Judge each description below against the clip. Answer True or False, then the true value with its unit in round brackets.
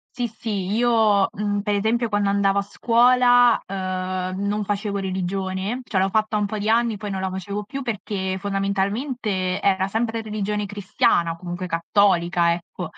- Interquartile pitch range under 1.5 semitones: False (2.5 semitones)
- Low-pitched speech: False (200 Hz)